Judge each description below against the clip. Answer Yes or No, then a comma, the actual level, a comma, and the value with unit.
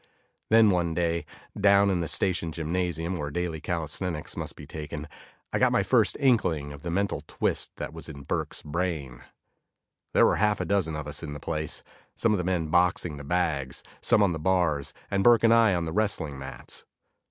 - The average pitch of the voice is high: No, very low, 85 Hz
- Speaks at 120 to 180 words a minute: No, average, 200 wpm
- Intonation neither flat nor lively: Yes, average, 3.7 semitones